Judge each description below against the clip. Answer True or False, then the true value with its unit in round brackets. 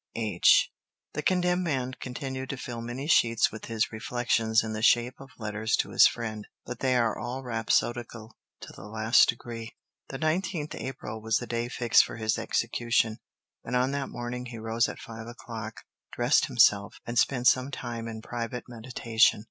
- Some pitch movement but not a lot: False (2.2 semitones)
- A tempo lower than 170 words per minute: False (175 wpm)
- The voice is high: False (120 Hz)